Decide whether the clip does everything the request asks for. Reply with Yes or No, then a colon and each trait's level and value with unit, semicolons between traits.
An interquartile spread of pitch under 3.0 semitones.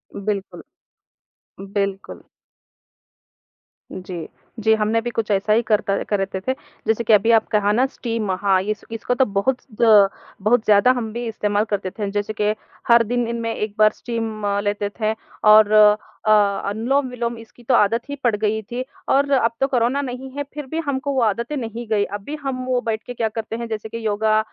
Yes: narrow, 2.5 semitones